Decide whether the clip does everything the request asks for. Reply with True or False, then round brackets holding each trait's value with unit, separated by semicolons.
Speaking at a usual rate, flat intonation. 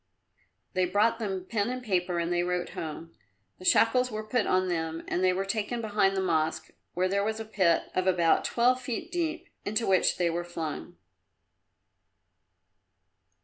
False (170 wpm; 4.0 semitones)